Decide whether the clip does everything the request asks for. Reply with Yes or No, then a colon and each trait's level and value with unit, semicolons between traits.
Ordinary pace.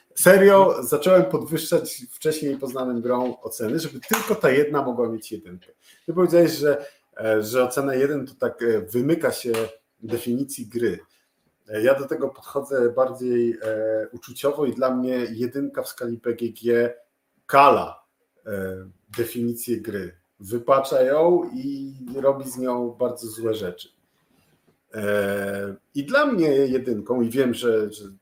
Yes: average, 125 wpm